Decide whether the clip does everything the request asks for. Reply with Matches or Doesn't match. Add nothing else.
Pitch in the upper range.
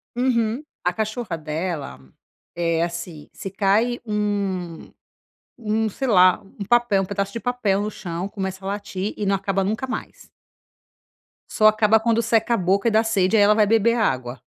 Matches